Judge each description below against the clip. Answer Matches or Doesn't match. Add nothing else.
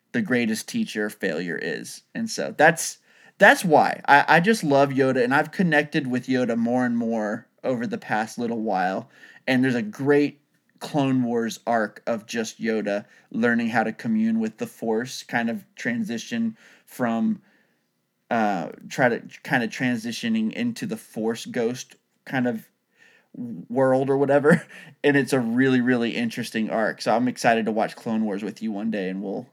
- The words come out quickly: Doesn't match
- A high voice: Doesn't match